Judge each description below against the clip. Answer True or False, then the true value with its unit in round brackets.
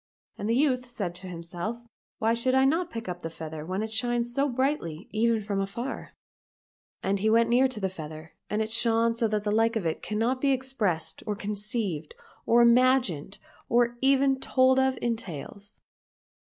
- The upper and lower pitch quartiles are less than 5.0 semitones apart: True (4.3 semitones)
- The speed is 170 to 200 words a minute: True (195 wpm)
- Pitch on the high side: True (225 Hz)